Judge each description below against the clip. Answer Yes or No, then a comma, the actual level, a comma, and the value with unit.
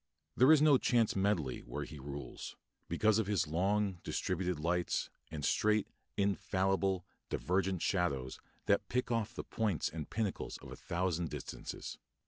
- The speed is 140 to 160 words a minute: Yes, average, 145 wpm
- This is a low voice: Yes, very low, 95 Hz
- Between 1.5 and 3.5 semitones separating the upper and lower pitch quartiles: No, average, 4.0 semitones